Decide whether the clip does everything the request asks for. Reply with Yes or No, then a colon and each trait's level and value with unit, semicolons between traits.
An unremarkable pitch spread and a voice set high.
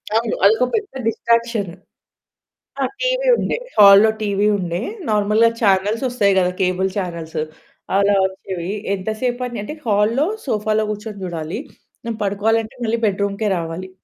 Yes: average, 3.1 semitones; high, 210 Hz